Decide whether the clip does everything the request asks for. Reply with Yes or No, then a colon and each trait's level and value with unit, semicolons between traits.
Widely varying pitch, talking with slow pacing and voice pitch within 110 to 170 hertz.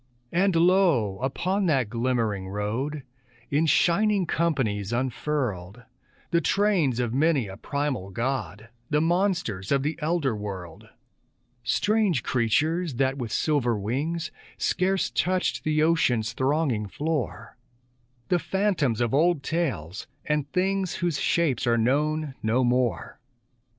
Yes: wide, 6.5 semitones; slow, 120 wpm; medium, 140 Hz